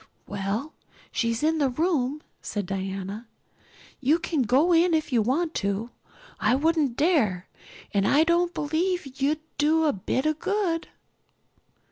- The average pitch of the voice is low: No, very high, 290 Hz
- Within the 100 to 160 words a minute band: Yes, average, 140 wpm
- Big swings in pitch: Yes, wide, 6.2 semitones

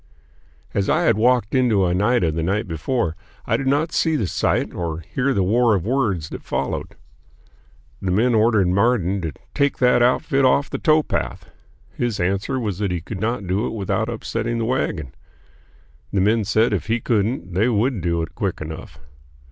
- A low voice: Yes, low, 110 Hz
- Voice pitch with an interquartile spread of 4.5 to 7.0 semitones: Yes, average, 5.1 semitones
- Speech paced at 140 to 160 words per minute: No, average, 180 wpm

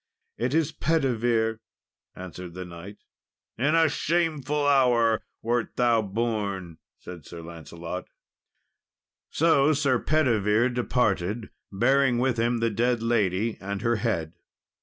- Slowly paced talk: Yes, slow, 115 wpm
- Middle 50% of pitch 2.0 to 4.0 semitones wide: No, average, 4.9 semitones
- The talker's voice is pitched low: Yes, low, 115 Hz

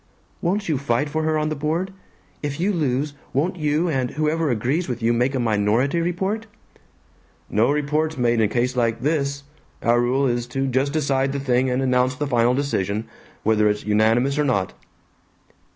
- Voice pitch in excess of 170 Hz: No, low, 135 Hz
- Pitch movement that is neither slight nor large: Yes, average, 4.0 semitones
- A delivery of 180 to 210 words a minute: Yes, average, 185 wpm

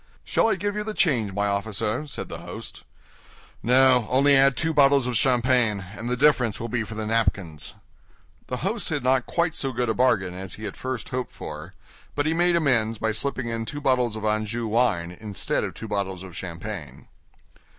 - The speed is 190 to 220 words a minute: Yes, average, 200 wpm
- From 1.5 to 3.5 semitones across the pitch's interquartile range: No, average, 4.2 semitones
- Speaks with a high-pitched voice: No, low, 120 Hz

